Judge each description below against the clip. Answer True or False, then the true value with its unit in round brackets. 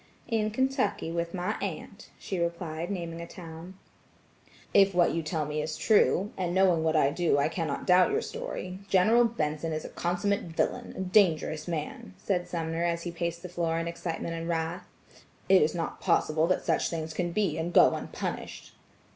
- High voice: False (170 Hz)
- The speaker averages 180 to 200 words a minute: True (185 wpm)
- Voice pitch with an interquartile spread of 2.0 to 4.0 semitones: True (2.4 semitones)